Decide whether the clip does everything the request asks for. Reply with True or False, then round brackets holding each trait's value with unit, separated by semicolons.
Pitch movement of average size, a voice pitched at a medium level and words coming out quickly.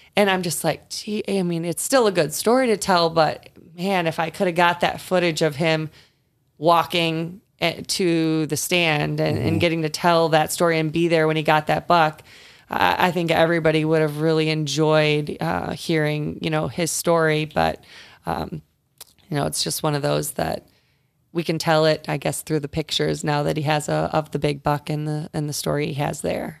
False (2.0 semitones; 160 Hz; 210 wpm)